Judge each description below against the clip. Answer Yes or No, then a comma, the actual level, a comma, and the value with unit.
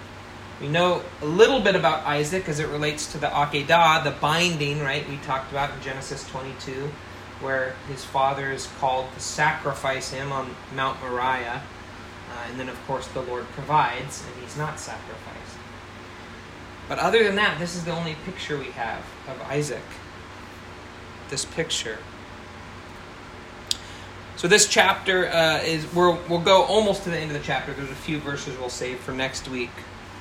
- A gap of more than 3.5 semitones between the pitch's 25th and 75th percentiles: Yes, average, 4.4 semitones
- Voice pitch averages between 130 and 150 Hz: Yes, low, 135 Hz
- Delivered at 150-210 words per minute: Yes, average, 165 wpm